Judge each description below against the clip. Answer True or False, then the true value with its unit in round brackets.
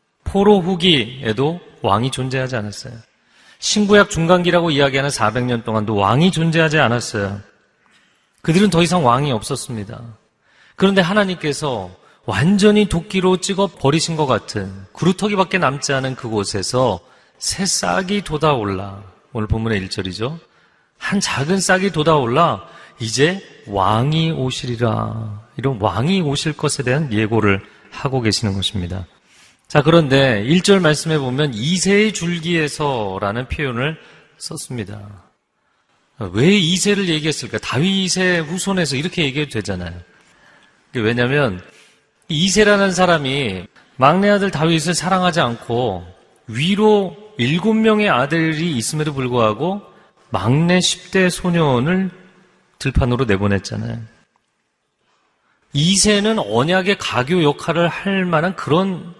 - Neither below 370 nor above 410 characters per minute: False (275 characters per minute)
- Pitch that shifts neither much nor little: False (8.2 semitones)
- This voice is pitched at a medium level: True (145 Hz)